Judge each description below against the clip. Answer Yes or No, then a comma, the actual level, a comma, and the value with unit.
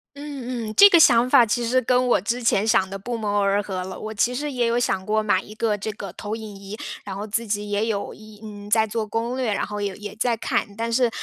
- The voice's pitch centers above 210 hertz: Yes, high, 220 Hz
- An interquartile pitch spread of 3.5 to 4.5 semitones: No, average, 2.7 semitones